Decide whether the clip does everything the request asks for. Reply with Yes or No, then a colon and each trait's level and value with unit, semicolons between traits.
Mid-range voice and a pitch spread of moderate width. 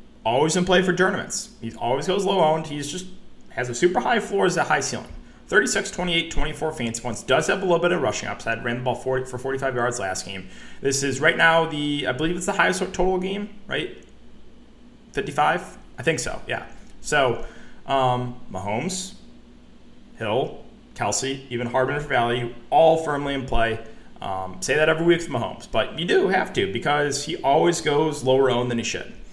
No: medium, 145 Hz; wide, 6.1 semitones